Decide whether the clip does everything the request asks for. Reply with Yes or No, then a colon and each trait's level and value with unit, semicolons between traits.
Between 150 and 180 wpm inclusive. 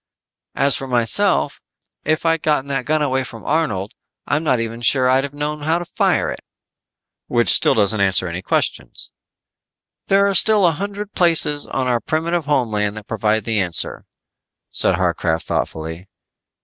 Yes: average, 165 wpm